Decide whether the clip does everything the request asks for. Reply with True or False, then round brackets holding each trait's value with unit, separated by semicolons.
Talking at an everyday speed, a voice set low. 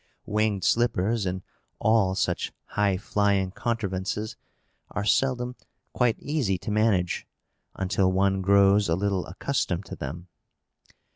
False (120 wpm; 100 Hz)